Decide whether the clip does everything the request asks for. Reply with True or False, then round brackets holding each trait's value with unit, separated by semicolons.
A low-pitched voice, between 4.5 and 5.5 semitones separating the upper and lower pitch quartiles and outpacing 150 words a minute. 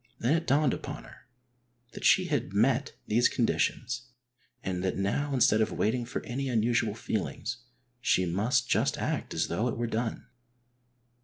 False (120 Hz; 3.0 semitones; 160 wpm)